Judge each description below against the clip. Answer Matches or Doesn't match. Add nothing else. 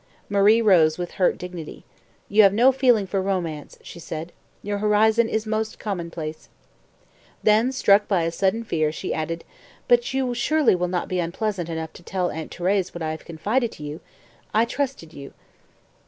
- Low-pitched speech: Doesn't match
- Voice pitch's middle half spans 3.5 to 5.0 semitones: Matches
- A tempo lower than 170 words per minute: Doesn't match